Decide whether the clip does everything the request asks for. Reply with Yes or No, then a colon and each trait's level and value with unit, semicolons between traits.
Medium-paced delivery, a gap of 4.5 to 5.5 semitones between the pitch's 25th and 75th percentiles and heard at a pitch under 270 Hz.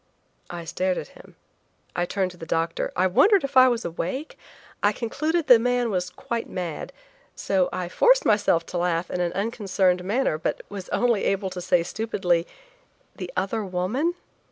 Yes: average, 180 wpm; average, 4.9 semitones; high, 190 Hz